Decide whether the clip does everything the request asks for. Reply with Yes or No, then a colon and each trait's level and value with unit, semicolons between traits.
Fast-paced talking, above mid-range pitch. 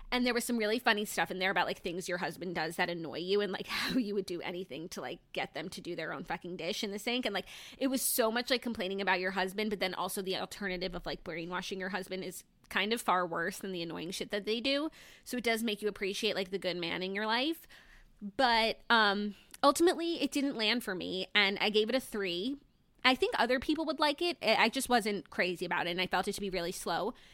Yes: fast, 260 wpm; high, 205 Hz